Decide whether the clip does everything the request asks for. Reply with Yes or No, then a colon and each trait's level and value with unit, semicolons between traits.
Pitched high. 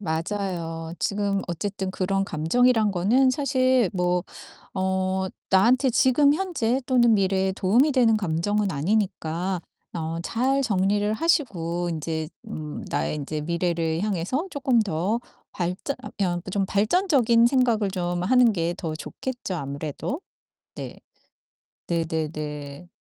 Yes: high, 195 Hz